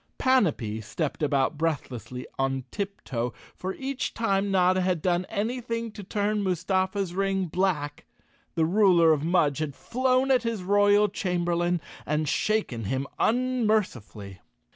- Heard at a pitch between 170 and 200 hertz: Yes, medium, 185 Hz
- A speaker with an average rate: No, slow, 130 wpm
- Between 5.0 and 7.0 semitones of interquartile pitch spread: Yes, wide, 5.6 semitones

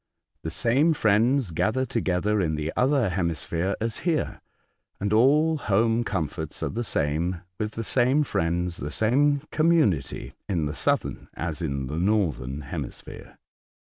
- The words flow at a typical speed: Yes, average, 145 wpm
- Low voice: Yes, low, 100 Hz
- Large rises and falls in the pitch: Yes, wide, 7.3 semitones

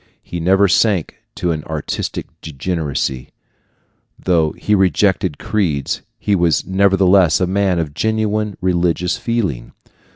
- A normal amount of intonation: Yes, average, 3.9 semitones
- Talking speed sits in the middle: No, slow, 120 wpm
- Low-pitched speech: Yes, very low, 90 Hz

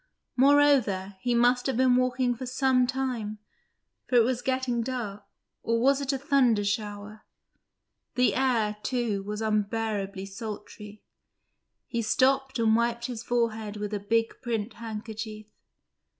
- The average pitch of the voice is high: Yes, high, 230 Hz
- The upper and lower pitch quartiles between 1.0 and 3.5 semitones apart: Yes, average, 3.1 semitones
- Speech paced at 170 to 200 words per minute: No, slow, 135 wpm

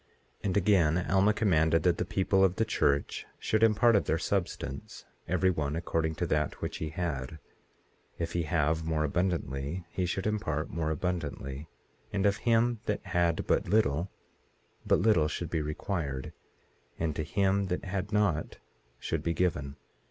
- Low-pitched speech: Yes, very low, 85 Hz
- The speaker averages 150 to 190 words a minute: Yes, average, 165 wpm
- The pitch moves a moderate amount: Yes, average, 4.0 semitones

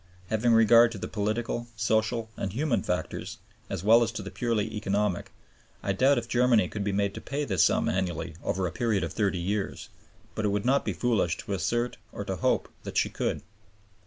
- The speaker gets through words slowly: No, fast, 205 wpm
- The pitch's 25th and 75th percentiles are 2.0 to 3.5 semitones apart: Yes, average, 3.1 semitones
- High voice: No, low, 110 Hz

